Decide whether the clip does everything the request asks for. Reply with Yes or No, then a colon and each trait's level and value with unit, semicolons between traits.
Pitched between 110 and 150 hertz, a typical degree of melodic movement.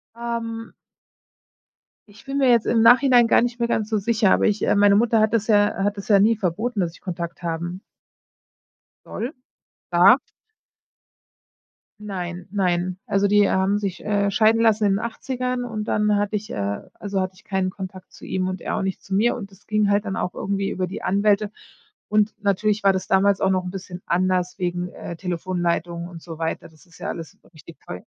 No: high, 200 Hz; average, 3.0 semitones